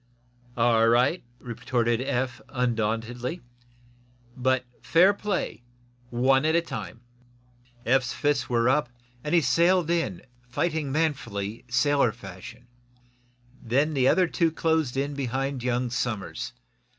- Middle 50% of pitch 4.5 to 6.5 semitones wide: No, average, 4.0 semitones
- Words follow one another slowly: Yes, slow, 115 wpm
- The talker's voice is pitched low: Yes, low, 130 Hz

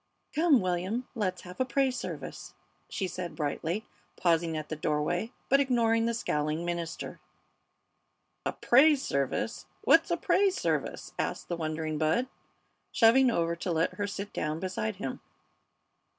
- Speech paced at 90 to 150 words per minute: Yes, average, 145 wpm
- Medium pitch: Yes, medium, 180 Hz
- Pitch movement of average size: No, wide, 6.7 semitones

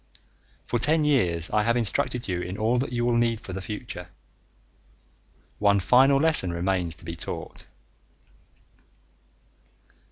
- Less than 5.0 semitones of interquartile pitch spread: No, average, 5.3 semitones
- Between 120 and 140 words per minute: Yes, slow, 135 wpm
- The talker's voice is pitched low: Yes, low, 110 Hz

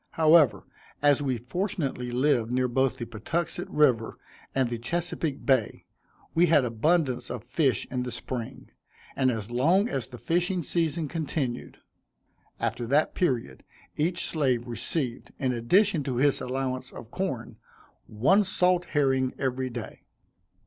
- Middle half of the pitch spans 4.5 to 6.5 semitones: Yes, average, 4.9 semitones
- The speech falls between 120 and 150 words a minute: Yes, average, 140 wpm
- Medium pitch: No, low, 130 Hz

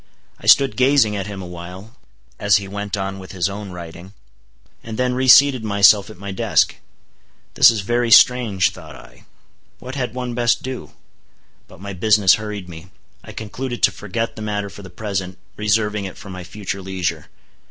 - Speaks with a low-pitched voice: Yes, low, 105 Hz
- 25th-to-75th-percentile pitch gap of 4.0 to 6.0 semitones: No, average, 3.3 semitones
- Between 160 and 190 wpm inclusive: Yes, average, 175 wpm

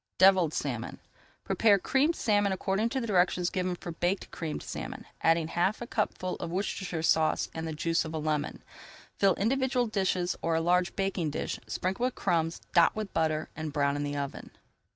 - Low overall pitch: No, medium, 180 Hz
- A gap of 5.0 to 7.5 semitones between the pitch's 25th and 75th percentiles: No, average, 3.7 semitones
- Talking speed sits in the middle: Yes, average, 180 wpm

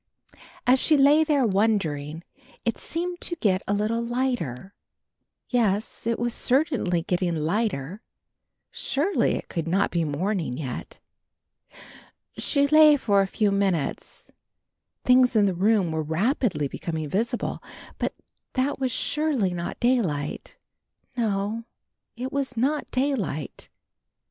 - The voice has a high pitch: Yes, high, 215 Hz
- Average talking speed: No, slow, 125 wpm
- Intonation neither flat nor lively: No, wide, 6.7 semitones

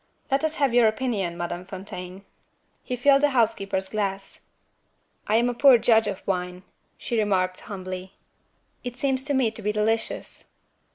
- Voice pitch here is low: No, high, 215 Hz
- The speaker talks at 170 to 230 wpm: No, average, 160 wpm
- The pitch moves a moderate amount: Yes, average, 4.5 semitones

